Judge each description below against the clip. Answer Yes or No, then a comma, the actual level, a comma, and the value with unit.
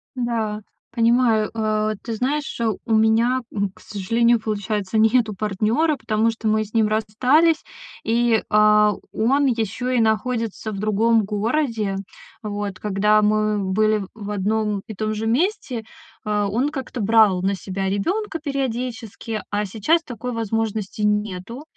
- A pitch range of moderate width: No, narrow, 2.2 semitones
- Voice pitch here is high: Yes, high, 220 Hz